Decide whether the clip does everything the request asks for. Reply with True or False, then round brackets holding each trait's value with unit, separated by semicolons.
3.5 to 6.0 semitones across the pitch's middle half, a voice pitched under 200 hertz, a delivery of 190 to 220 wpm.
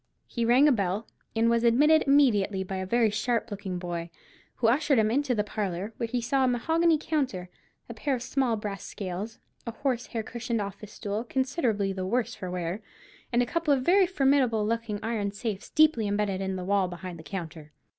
False (4.5 semitones; 225 Hz; 200 wpm)